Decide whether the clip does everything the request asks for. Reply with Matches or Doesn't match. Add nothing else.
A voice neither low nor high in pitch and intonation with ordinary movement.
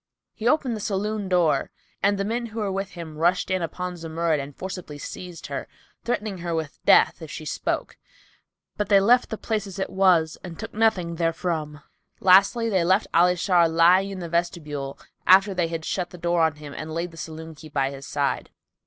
Matches